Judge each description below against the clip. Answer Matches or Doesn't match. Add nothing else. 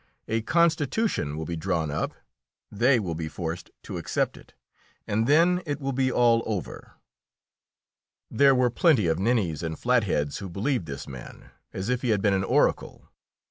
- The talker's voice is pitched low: Matches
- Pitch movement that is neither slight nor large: Doesn't match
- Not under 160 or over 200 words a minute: Matches